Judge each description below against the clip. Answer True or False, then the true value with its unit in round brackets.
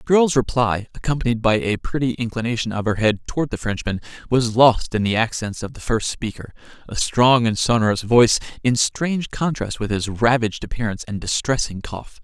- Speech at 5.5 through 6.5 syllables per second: True (5.6 syllables/s)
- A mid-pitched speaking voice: False (115 Hz)